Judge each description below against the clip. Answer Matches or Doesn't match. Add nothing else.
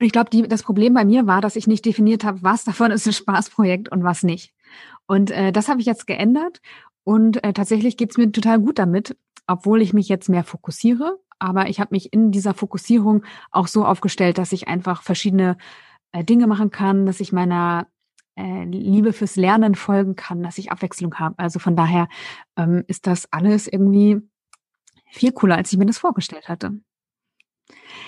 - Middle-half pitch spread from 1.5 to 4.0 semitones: Matches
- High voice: Matches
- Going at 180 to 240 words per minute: Matches